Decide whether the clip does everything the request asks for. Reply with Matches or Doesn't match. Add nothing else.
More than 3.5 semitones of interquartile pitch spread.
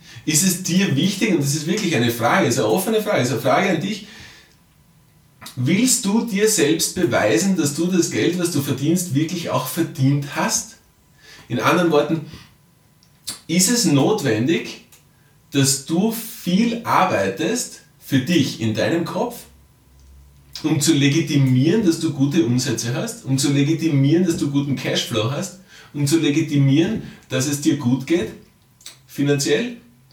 Matches